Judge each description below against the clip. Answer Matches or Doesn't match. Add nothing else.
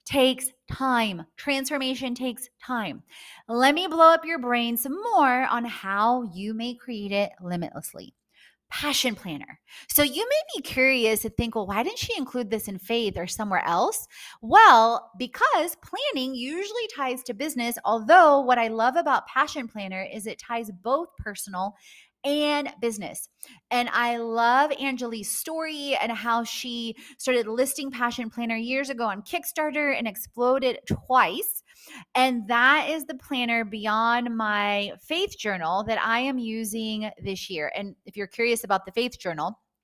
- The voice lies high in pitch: Matches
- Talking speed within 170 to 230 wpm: Doesn't match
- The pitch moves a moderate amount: Matches